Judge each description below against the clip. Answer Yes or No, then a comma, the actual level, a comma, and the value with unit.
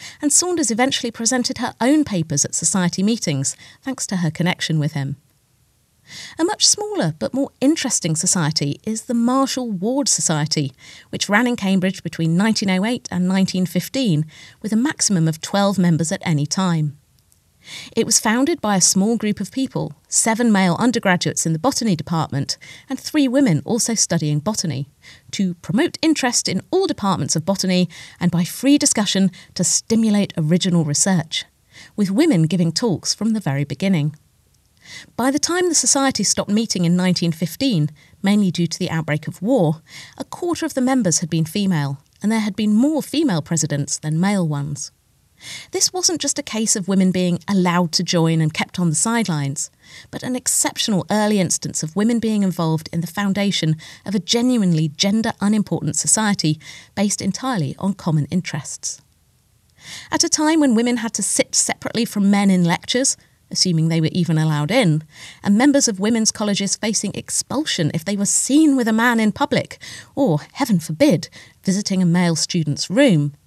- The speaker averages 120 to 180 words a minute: Yes, average, 170 wpm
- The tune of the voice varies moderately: No, wide, 6.4 semitones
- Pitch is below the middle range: No, high, 190 Hz